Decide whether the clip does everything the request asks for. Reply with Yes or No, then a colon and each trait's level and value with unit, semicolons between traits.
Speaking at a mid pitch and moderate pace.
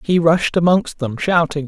Yes: medium, 165 Hz; average, 180 wpm